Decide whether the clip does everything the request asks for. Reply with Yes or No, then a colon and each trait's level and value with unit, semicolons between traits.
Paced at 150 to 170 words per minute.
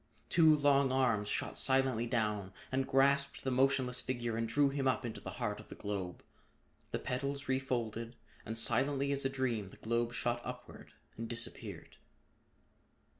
Yes: average, 160 wpm